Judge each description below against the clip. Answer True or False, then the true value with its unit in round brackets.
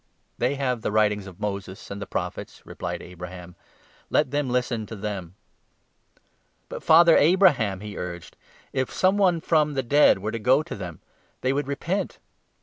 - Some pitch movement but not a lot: False (6.8 semitones)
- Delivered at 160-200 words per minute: True (185 wpm)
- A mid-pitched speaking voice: False (115 Hz)